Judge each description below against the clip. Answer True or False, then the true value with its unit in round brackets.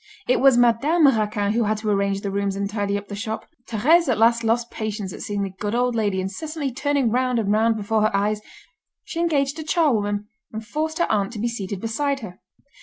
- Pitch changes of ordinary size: True (3.9 semitones)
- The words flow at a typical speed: False (220 wpm)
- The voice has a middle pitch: False (220 Hz)